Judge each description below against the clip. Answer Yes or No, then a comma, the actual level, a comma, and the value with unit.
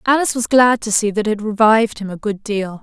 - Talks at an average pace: No, fast, 255 wpm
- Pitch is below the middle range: No, high, 215 Hz